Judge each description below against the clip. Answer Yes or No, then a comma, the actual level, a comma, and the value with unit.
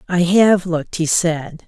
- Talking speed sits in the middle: Yes, average, 180 wpm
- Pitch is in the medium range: Yes, medium, 175 Hz